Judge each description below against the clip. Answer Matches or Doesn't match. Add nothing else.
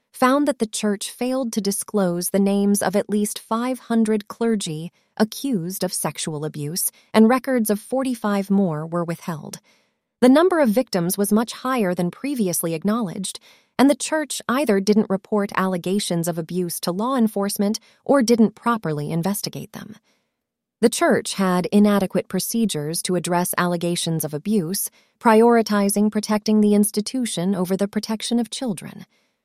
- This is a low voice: Doesn't match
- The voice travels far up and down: Doesn't match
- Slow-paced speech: Doesn't match